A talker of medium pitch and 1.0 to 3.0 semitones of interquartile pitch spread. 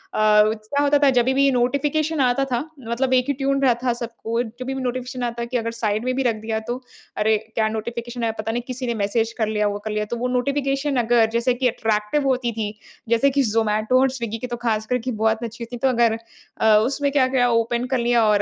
No: high, 240 Hz; narrow, 2.6 semitones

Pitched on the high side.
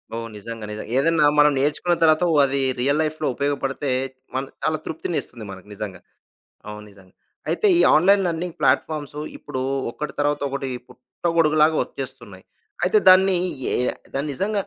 No: medium, 145 Hz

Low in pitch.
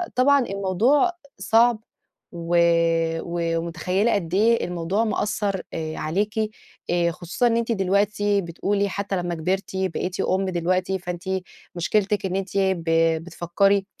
No: high, 190 Hz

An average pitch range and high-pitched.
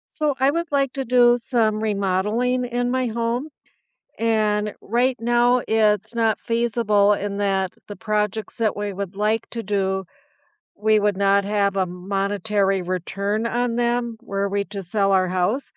Yes: average, 3.2 semitones; high, 215 Hz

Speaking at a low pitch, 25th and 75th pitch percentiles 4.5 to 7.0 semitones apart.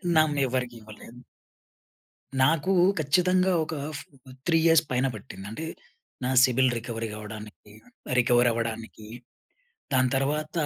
Yes: low, 130 Hz; average, 5.2 semitones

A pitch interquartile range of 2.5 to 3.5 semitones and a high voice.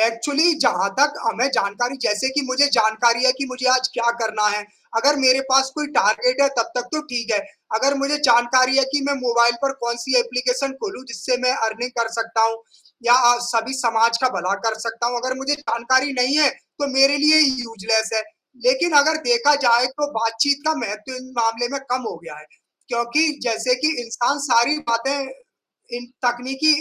Yes: average, 2.8 semitones; high, 245 Hz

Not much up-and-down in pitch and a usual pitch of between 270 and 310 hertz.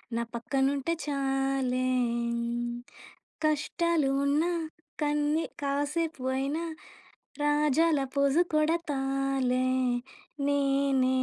Yes: narrow, 2.1 semitones; very high, 280 Hz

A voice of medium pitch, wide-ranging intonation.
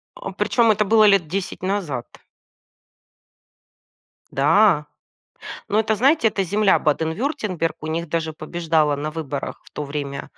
Yes: medium, 170 Hz; wide, 5.7 semitones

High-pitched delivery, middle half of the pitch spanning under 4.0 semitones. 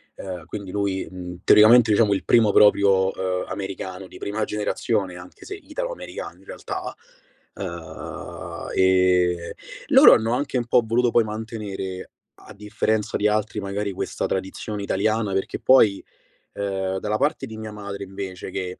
No: low, 100 Hz; narrow, 2.5 semitones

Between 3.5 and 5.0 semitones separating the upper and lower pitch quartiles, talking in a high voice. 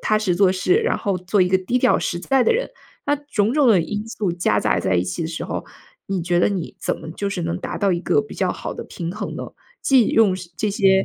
Yes: average, 4.2 semitones; high, 195 Hz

